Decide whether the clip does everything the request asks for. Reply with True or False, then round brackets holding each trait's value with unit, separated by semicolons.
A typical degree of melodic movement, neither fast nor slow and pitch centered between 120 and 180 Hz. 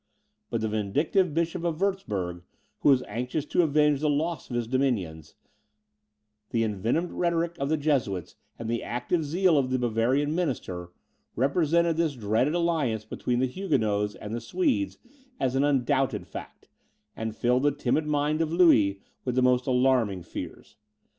False (5.8 semitones; 160 wpm; 135 Hz)